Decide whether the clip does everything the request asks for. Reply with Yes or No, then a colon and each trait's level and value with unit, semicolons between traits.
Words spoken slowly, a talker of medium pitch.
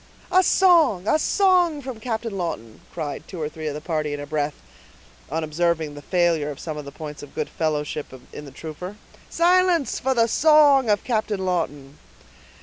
No: average, 185 wpm; medium, 175 Hz